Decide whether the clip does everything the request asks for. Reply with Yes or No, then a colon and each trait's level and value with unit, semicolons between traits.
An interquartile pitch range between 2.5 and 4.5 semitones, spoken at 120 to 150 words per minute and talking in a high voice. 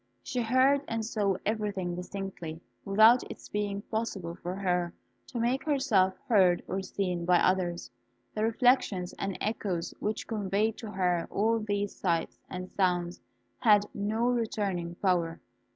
Yes: average, 3.6 semitones; average, 140 wpm; high, 200 Hz